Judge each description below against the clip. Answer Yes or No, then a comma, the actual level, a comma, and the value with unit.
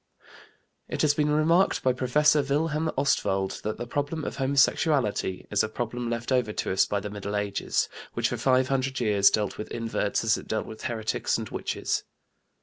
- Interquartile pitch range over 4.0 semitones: Yes, average, 5.0 semitones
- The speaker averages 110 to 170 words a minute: No, average, 185 wpm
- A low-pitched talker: Yes, low, 120 Hz